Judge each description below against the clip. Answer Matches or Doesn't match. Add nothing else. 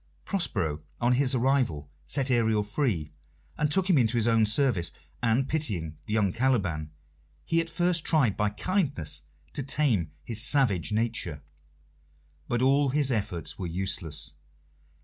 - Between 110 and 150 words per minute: Matches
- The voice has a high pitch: Doesn't match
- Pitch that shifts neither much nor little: Doesn't match